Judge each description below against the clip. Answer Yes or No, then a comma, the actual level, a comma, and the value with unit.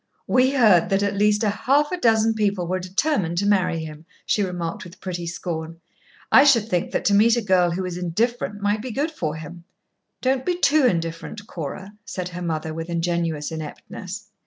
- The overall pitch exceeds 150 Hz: Yes, high, 190 Hz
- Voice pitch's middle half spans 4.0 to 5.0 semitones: Yes, average, 4.6 semitones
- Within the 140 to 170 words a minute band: No, average, 190 wpm